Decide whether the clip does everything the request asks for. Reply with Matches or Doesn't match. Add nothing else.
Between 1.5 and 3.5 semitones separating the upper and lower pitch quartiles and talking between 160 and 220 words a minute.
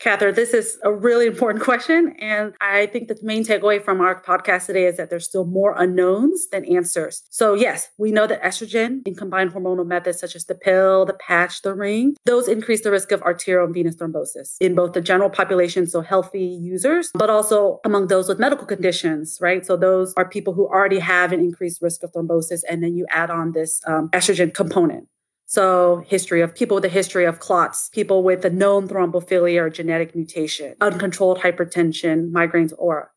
Matches